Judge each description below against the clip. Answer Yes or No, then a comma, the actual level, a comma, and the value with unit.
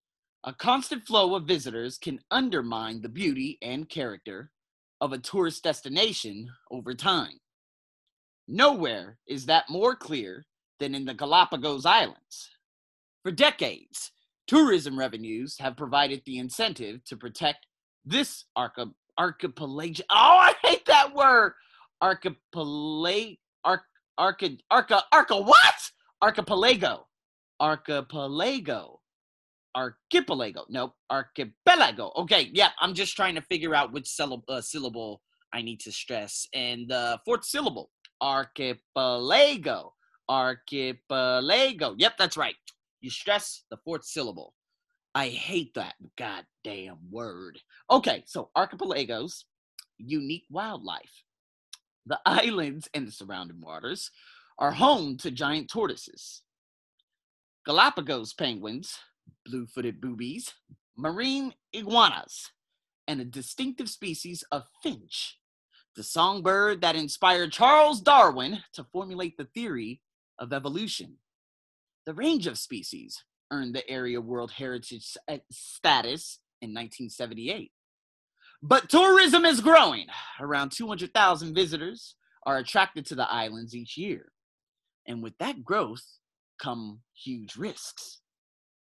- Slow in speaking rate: Yes, slow, 115 wpm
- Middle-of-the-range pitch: Yes, medium, 150 Hz